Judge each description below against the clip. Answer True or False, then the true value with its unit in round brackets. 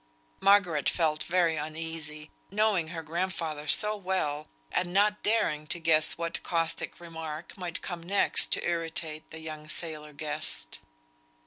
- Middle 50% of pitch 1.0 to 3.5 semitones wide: True (2.6 semitones)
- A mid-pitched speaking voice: True (165 Hz)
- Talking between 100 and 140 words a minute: True (135 wpm)